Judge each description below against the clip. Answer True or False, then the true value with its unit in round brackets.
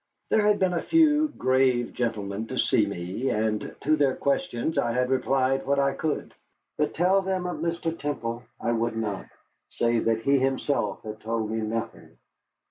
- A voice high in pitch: False (130 Hz)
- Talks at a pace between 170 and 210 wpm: True (175 wpm)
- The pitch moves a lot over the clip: True (5.9 semitones)